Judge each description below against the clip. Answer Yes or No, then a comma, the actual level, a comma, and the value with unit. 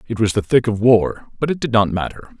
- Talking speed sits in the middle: No, fast, 275 wpm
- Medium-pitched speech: No, low, 110 Hz